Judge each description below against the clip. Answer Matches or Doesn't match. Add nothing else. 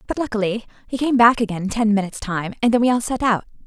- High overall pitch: Matches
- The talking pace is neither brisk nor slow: Doesn't match